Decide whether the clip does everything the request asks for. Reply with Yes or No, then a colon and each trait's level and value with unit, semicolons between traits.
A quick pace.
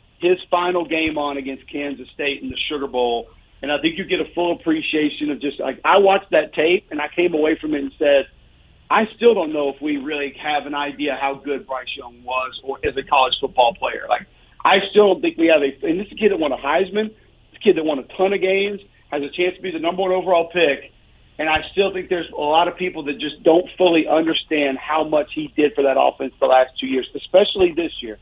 Yes: fast, 255 wpm